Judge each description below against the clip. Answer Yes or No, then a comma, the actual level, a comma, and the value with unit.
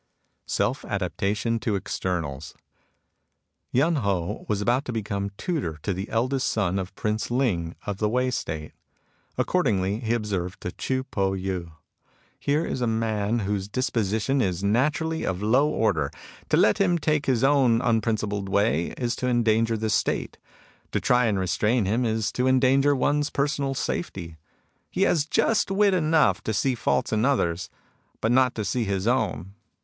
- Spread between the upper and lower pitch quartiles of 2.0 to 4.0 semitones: No, average, 4.9 semitones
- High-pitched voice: No, low, 110 Hz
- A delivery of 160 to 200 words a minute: Yes, average, 165 wpm